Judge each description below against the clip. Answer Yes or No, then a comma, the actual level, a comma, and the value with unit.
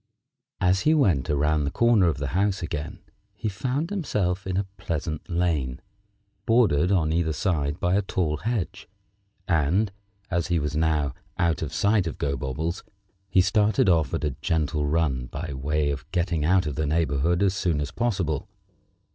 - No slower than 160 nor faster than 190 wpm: Yes, average, 170 wpm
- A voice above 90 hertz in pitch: No, very low, 85 Hz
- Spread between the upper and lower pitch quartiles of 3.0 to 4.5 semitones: Yes, average, 4.2 semitones